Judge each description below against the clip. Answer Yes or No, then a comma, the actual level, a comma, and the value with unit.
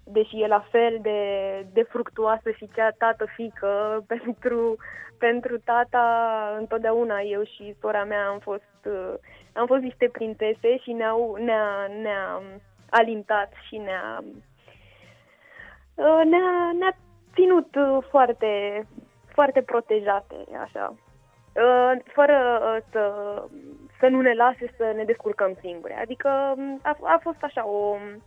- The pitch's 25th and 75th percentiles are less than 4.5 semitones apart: Yes, average, 3.0 semitones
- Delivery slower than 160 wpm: Yes, slow, 115 wpm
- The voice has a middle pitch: No, high, 225 Hz